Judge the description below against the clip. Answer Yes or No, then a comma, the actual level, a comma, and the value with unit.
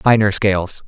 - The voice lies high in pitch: No, low, 100 Hz